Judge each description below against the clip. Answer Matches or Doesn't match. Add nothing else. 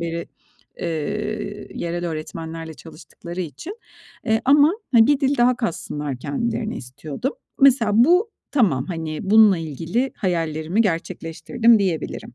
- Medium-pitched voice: Matches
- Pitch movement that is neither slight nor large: Doesn't match